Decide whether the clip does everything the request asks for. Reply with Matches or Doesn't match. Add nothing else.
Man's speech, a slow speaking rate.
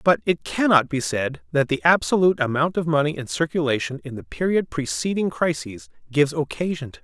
Doesn't match